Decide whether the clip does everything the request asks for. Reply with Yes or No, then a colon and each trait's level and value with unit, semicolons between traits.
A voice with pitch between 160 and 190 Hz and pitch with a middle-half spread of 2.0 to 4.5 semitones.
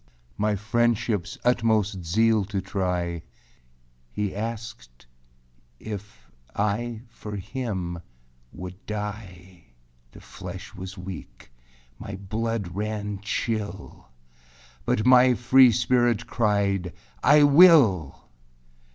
No: low, 105 Hz; average, 3.6 semitones